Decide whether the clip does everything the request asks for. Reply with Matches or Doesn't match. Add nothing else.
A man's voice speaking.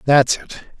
Matches